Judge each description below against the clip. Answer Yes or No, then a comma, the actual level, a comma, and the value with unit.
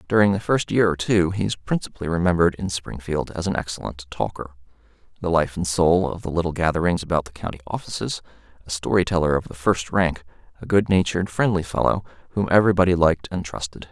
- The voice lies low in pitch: Yes, very low, 85 Hz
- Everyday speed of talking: Yes, average, 190 wpm